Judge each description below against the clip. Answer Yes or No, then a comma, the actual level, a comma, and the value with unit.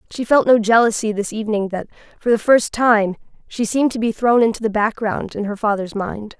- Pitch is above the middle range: Yes, high, 220 Hz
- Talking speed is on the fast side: Yes, fast, 215 wpm